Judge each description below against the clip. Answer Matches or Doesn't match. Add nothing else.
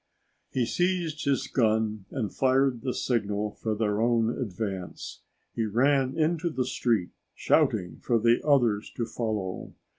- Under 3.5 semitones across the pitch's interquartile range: Doesn't match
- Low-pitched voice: Matches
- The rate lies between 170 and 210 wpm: Doesn't match